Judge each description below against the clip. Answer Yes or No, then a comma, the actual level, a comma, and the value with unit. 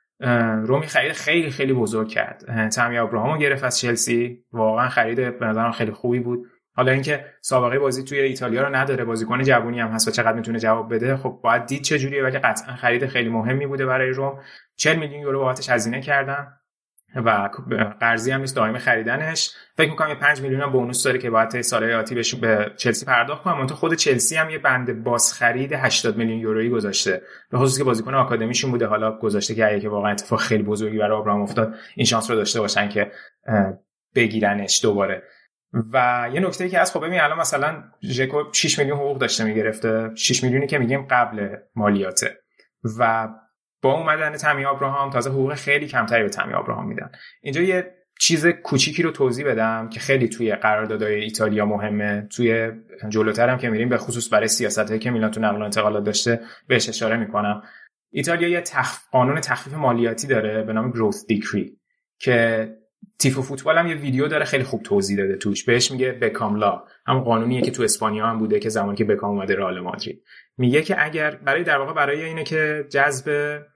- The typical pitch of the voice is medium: No, low, 120 Hz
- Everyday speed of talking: No, fast, 185 wpm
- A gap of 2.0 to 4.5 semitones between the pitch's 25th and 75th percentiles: Yes, average, 3.9 semitones